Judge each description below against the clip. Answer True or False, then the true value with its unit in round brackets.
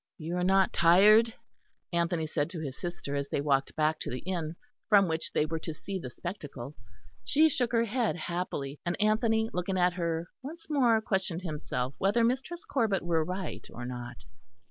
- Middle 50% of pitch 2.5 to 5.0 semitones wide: False (5.6 semitones)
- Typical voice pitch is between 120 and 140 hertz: False (175 Hz)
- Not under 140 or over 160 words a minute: False (185 wpm)